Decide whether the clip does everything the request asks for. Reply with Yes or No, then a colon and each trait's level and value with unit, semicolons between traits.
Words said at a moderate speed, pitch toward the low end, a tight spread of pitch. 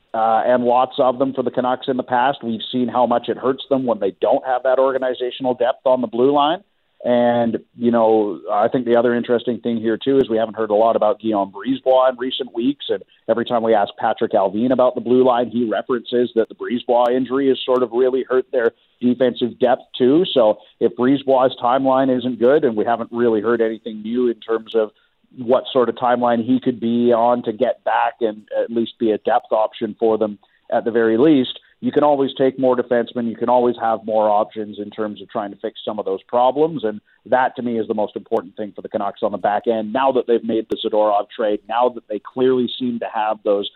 No: fast, 235 wpm; low, 120 Hz; narrow, 2.3 semitones